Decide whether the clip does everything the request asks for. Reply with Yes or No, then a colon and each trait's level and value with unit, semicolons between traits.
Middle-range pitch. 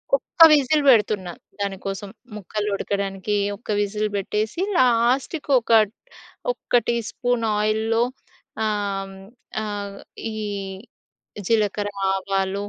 No: high, 210 Hz